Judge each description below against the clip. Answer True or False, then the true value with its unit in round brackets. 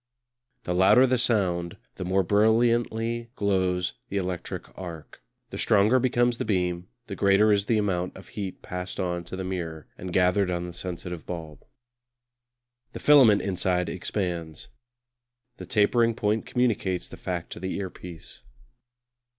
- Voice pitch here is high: False (95 Hz)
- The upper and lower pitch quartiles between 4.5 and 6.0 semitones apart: False (3.2 semitones)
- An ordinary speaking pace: True (145 wpm)